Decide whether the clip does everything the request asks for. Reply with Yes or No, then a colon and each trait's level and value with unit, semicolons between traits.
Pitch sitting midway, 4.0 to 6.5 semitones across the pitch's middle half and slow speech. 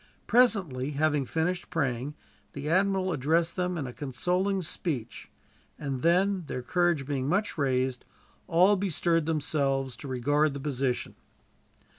Yes: medium, 150 Hz; average, 4.9 semitones; slow, 130 wpm